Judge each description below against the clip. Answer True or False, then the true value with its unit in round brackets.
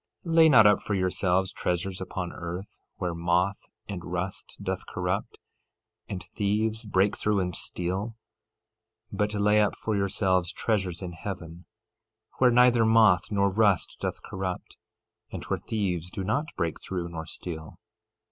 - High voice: False (95 Hz)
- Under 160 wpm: True (150 wpm)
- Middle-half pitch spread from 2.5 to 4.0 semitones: True (2.9 semitones)